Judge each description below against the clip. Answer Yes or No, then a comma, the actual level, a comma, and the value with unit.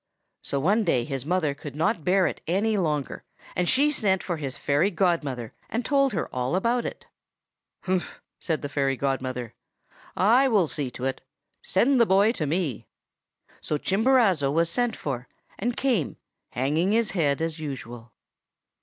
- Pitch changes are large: Yes, wide, 6.8 semitones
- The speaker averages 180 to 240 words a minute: No, average, 165 wpm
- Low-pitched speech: No, medium, 170 Hz